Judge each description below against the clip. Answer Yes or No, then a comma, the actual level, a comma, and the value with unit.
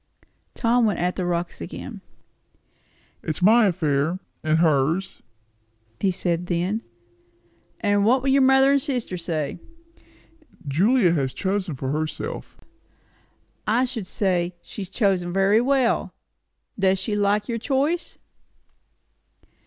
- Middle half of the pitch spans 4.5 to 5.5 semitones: Yes, average, 5.1 semitones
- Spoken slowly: Yes, slow, 120 wpm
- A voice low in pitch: No, high, 195 Hz